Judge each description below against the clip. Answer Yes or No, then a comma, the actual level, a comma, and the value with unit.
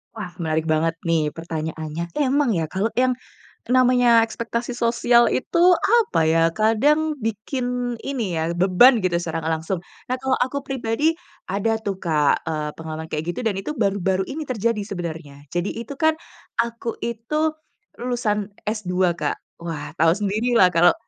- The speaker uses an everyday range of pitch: No, wide, 6.7 semitones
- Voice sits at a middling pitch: No, high, 210 Hz